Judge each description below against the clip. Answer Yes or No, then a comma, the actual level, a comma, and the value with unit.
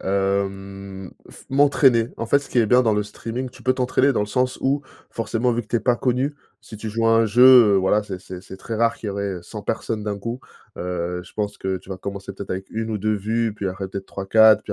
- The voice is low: Yes, low, 105 Hz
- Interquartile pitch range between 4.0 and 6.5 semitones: No, average, 3.2 semitones